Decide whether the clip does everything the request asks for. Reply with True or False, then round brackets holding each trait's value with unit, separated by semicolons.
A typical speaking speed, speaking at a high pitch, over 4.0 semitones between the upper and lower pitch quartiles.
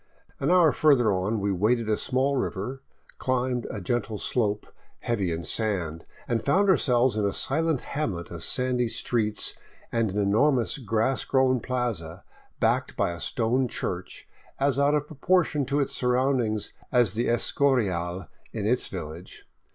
False (150 wpm; 120 Hz; 4.5 semitones)